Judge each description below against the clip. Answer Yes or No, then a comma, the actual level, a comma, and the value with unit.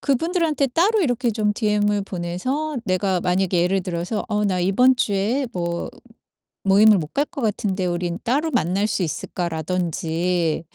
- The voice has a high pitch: Yes, high, 195 Hz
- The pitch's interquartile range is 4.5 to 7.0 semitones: Yes, wide, 5.6 semitones